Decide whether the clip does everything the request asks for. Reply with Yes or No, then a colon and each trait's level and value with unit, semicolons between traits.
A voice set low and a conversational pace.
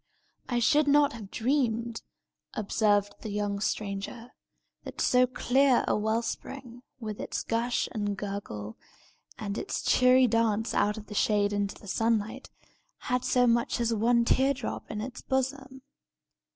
No: high, 230 Hz; average, 150 wpm